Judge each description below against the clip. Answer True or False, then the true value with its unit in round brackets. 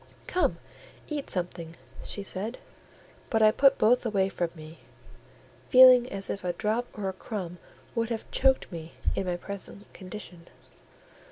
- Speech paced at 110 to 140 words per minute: False (150 wpm)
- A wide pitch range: False (4.7 semitones)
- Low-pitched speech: False (200 Hz)